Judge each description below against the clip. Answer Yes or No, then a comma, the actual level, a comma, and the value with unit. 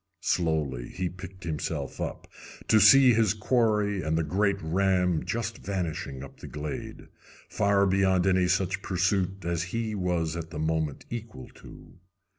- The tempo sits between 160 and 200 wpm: No, average, 150 wpm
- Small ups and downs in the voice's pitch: No, average, 3.4 semitones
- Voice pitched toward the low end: Yes, very low, 90 Hz